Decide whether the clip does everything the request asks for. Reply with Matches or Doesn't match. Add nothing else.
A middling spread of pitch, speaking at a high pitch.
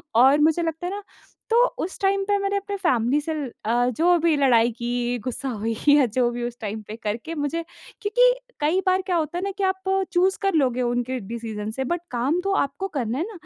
Doesn't match